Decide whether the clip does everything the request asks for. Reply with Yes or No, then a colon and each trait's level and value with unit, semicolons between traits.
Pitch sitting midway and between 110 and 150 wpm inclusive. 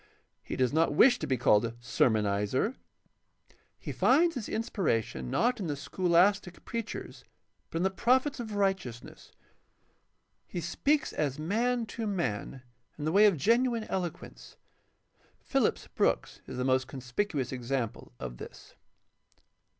Yes: medium, 170 Hz; slow, 135 wpm